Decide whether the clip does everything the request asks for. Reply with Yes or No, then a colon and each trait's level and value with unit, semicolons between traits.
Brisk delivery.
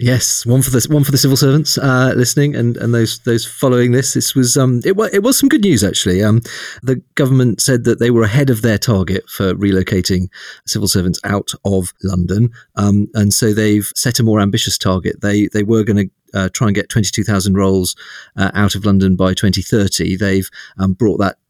Yes: fast, 220 wpm